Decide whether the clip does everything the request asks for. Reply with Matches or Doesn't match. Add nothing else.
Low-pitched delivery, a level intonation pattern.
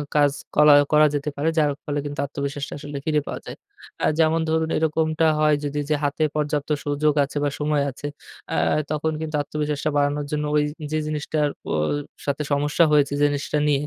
Doesn't match